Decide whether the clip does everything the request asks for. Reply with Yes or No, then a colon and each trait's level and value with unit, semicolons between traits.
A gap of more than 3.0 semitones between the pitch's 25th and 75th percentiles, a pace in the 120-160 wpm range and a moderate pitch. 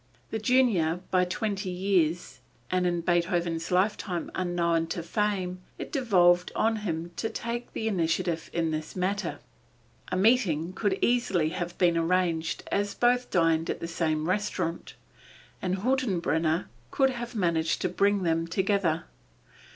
Yes: average, 3.5 semitones; average, 140 wpm; medium, 180 Hz